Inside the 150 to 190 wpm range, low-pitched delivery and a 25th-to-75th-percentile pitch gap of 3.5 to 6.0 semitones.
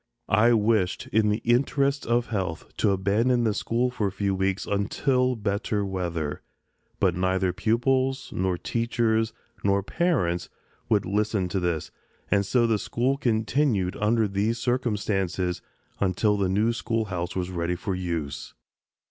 No: average, 140 wpm; low, 105 Hz; average, 3.9 semitones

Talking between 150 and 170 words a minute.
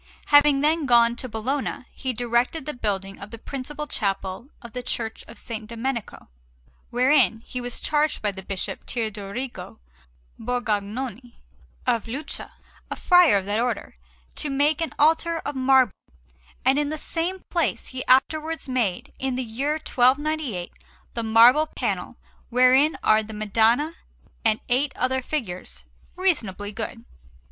No: average, 140 wpm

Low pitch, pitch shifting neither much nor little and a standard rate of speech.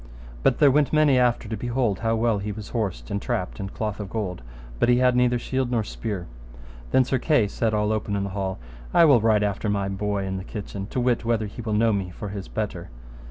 No: low, 110 Hz; average, 3.2 semitones; fast, 240 wpm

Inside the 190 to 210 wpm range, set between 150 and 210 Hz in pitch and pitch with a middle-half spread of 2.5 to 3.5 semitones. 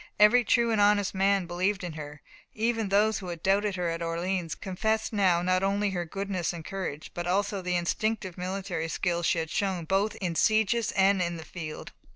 Yes: average, 195 wpm; high, 190 Hz; average, 2.9 semitones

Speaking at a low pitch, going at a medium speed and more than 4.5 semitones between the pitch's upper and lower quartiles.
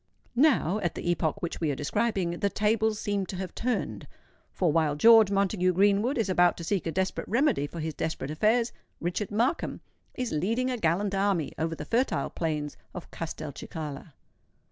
No: high, 190 Hz; average, 165 wpm; average, 4.9 semitones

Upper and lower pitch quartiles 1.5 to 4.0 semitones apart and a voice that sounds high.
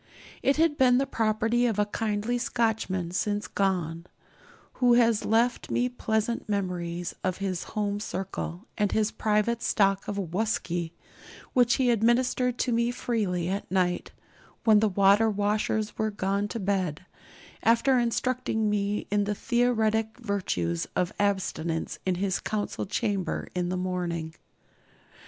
Yes: average, 3.7 semitones; high, 210 Hz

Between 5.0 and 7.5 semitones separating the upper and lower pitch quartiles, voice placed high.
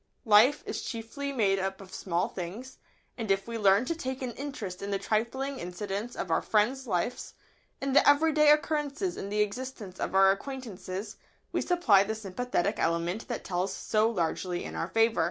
Yes: wide, 5.4 semitones; high, 220 Hz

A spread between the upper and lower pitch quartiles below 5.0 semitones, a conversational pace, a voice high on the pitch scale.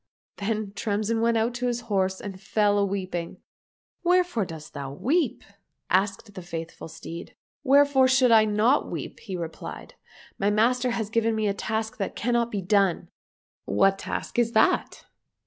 Yes: average, 3.6 semitones; average, 190 wpm; high, 215 Hz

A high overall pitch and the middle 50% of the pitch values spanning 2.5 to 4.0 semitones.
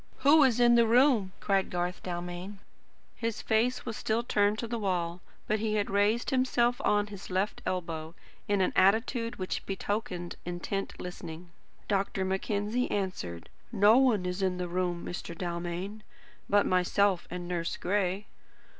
Yes: high, 195 Hz; average, 3.6 semitones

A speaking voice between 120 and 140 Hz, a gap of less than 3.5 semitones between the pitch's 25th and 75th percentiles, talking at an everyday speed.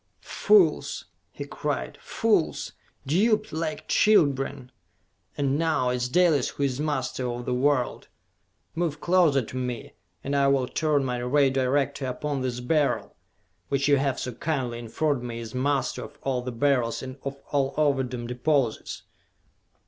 Yes: low, 135 Hz; average, 2.8 semitones; average, 150 wpm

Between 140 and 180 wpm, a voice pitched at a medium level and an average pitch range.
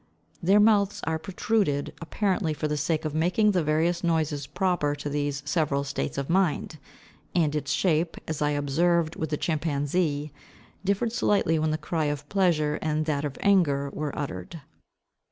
Yes: average, 165 wpm; medium, 155 Hz; average, 3.2 semitones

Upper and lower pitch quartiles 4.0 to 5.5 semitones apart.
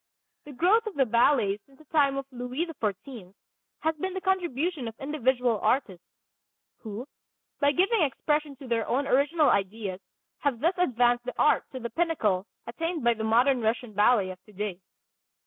Yes: average, 5.1 semitones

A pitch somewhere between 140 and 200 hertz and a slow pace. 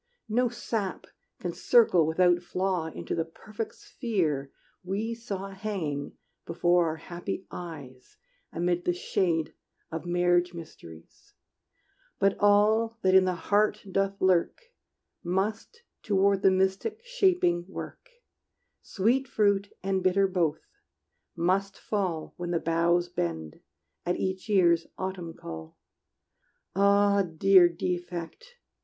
Yes: medium, 185 Hz; slow, 115 wpm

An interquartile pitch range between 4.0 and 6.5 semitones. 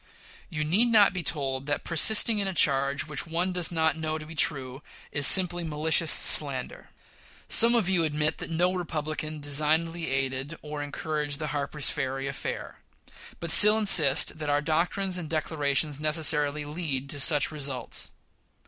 No: average, 2.7 semitones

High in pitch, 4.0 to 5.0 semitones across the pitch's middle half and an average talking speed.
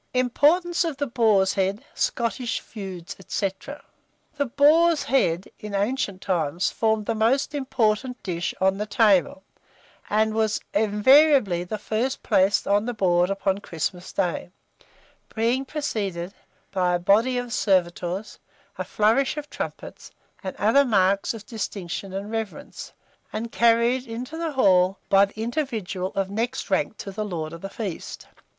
Yes: high, 215 Hz; average, 4.4 semitones; average, 145 wpm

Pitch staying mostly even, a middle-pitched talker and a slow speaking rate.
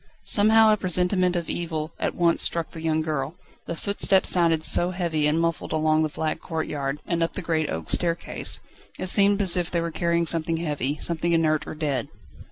No: narrow, 2.1 semitones; medium, 165 Hz; average, 195 wpm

